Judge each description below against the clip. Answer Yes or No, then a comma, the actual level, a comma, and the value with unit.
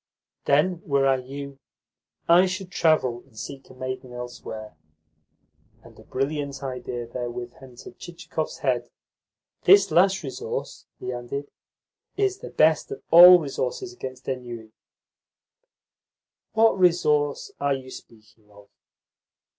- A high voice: No, low, 135 Hz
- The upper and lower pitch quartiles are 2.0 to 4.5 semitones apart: No, average, 5.3 semitones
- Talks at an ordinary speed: No, slow, 120 wpm